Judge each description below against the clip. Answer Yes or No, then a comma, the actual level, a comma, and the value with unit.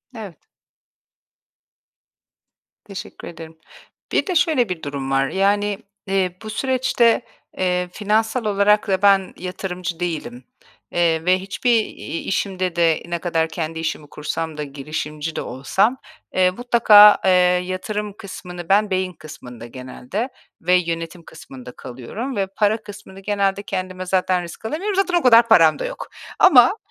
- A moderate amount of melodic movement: Yes, average, 4.3 semitones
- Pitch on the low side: No, medium, 185 Hz